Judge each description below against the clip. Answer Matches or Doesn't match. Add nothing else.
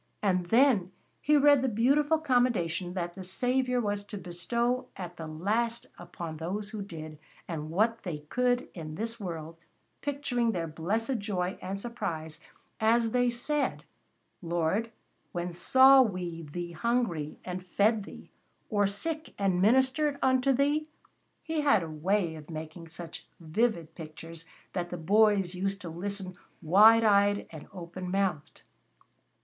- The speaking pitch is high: Matches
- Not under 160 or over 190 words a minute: Doesn't match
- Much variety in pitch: Matches